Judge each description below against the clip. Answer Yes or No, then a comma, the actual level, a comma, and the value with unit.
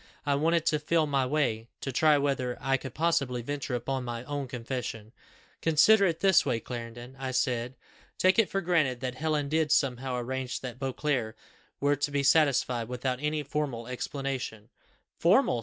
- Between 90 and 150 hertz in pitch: Yes, low, 135 Hz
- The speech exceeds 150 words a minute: Yes, average, 170 wpm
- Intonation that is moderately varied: Yes, average, 3.3 semitones